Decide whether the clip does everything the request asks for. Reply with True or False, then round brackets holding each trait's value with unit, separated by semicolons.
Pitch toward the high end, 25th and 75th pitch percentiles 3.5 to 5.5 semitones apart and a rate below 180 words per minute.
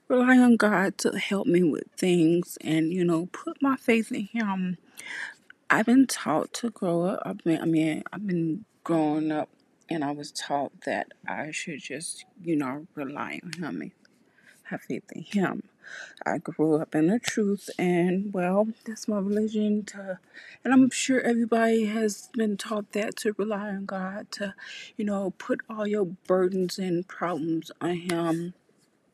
True (195 Hz; 4.5 semitones; 170 wpm)